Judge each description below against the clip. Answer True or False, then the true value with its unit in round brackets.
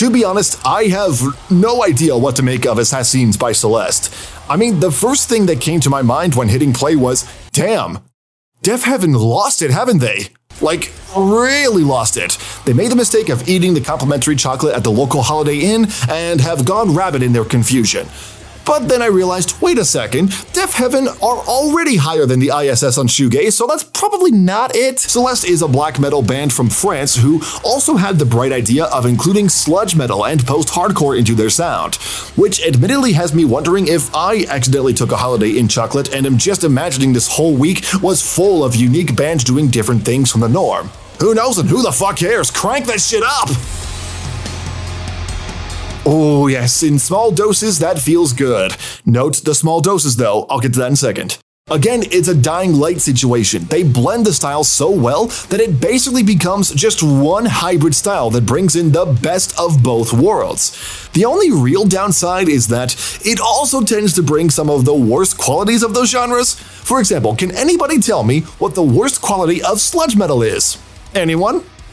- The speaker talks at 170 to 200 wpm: True (190 wpm)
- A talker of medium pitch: True (150 Hz)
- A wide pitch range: True (7.7 semitones)